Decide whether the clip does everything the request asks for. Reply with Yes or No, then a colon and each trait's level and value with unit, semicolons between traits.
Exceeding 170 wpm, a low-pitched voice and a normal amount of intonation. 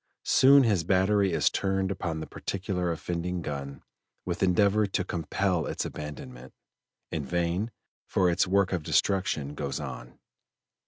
No: average, 140 wpm; very low, 90 Hz; average, 3.7 semitones